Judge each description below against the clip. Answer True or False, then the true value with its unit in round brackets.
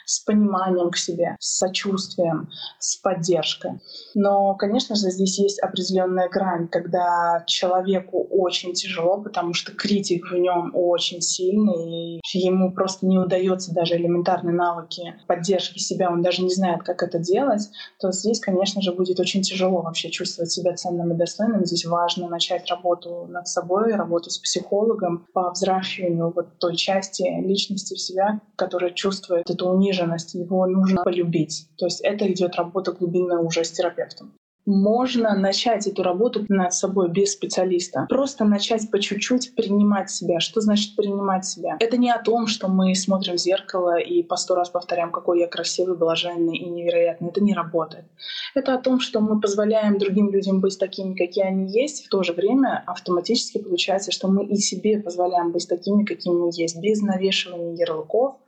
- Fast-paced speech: True (165 wpm)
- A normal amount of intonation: False (2.3 semitones)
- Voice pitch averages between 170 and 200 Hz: True (185 Hz)